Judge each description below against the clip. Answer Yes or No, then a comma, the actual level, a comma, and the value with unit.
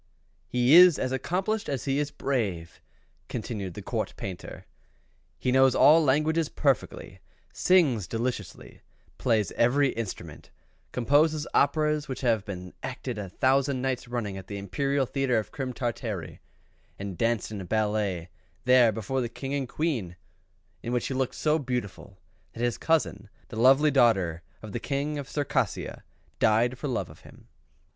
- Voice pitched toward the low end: Yes, low, 125 Hz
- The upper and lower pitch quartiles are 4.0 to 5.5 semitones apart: Yes, average, 4.7 semitones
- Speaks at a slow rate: No, average, 150 wpm